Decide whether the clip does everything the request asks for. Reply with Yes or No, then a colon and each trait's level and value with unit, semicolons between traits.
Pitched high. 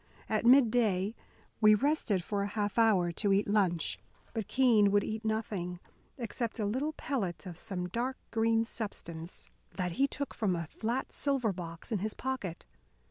Yes: high, 215 Hz